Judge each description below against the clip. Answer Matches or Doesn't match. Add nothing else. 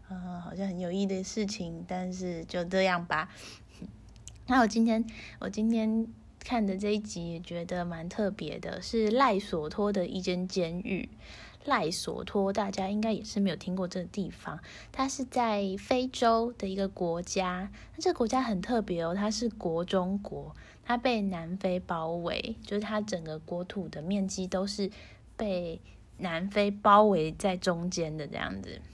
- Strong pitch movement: Doesn't match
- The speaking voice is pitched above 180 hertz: Matches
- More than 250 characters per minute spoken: Doesn't match